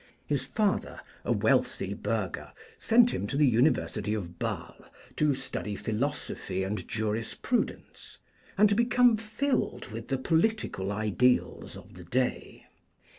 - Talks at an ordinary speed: No, slow, 125 wpm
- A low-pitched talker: Yes, low, 130 Hz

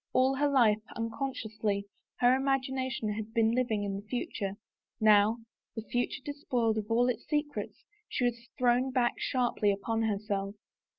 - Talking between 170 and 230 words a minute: No, average, 140 wpm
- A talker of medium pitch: No, high, 230 Hz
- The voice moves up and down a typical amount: Yes, average, 3.2 semitones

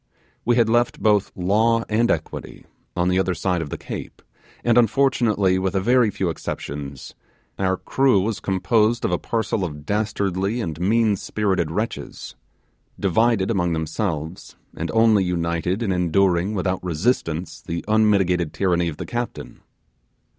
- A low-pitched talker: Yes, very low, 95 Hz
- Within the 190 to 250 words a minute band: No, average, 145 wpm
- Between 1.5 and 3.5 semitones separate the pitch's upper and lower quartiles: No, average, 4.0 semitones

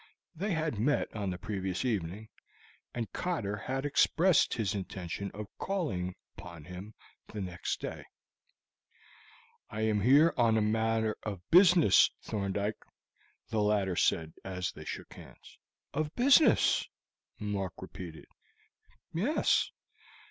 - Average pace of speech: No, slow, 120 wpm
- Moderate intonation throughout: No, wide, 6.3 semitones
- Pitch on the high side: No, low, 105 Hz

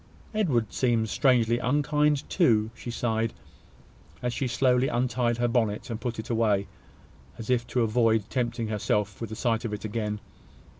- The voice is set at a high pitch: No, low, 115 Hz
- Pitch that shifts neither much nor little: No, narrow, 2.2 semitones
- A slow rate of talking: No, average, 160 wpm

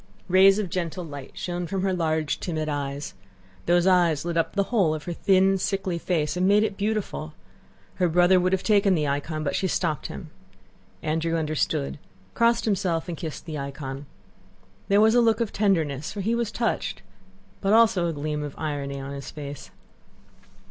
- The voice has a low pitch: No, medium, 175 Hz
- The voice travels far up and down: No, average, 4.3 semitones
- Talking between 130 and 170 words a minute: No, average, 185 wpm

